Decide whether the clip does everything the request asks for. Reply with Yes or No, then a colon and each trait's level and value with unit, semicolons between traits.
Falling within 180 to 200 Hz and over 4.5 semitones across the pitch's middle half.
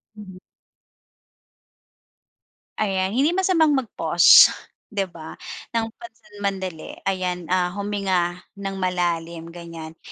No: high, 190 Hz; average, 3.2 semitones